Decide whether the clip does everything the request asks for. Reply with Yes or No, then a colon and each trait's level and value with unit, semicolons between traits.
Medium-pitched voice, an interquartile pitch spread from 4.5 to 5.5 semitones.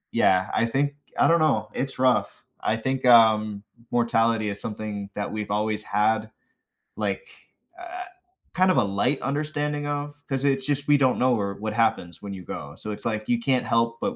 No: low, 115 Hz; average, 4.8 semitones